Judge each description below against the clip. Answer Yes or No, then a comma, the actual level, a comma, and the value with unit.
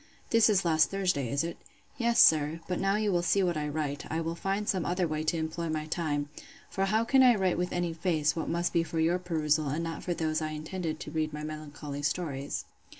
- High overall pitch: No, medium, 165 Hz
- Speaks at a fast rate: Yes, fast, 235 wpm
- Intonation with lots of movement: No, average, 2.9 semitones